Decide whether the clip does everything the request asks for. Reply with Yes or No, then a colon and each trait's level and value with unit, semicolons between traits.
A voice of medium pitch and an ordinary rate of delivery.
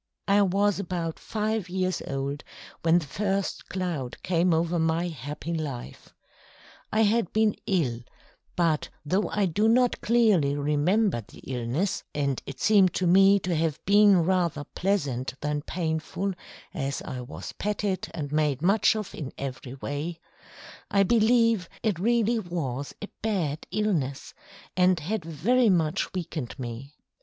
Yes: medium, 175 Hz; average, 145 wpm